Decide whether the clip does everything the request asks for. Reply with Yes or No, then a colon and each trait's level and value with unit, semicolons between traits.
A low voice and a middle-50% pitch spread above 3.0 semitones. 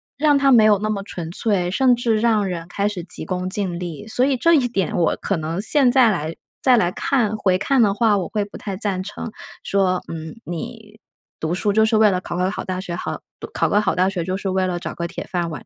No: high, 200 Hz; average, 3.5 semitones